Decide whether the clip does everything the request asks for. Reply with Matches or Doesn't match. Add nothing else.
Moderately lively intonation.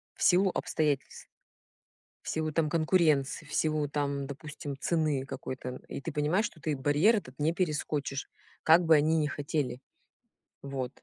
Doesn't match